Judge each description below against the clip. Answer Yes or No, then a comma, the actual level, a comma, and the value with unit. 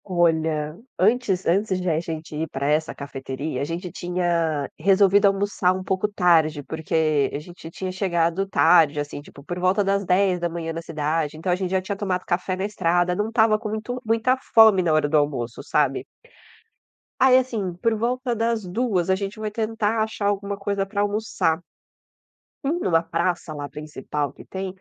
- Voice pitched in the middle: Yes, medium, 180 Hz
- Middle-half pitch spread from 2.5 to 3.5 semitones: No, average, 4.2 semitones